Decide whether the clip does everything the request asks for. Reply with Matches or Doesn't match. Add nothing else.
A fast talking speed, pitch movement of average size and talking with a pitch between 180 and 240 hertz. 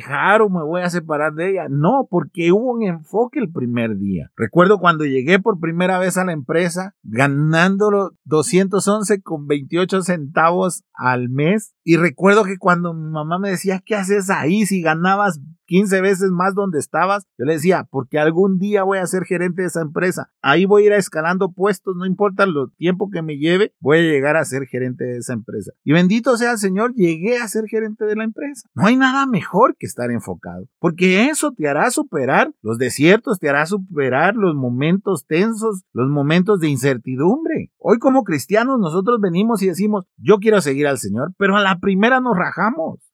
Matches